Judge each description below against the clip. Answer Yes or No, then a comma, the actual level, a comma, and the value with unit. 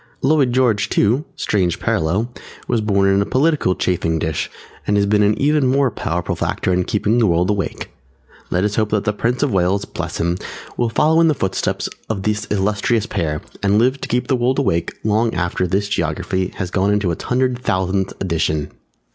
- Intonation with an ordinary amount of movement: Yes, average, 4.7 semitones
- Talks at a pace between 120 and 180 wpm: No, average, 195 wpm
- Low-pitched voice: Yes, low, 105 Hz